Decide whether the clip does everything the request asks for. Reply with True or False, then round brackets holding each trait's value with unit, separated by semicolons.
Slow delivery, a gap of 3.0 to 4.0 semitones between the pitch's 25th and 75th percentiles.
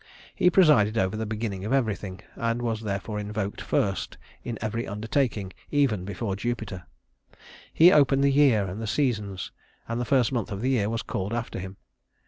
False (175 wpm; 3.4 semitones)